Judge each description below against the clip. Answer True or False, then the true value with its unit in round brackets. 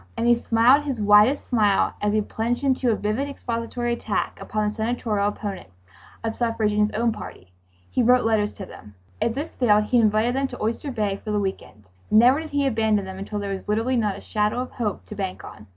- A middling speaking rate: False (225 wpm)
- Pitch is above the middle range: True (220 Hz)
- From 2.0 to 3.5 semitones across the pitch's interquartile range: True (2.7 semitones)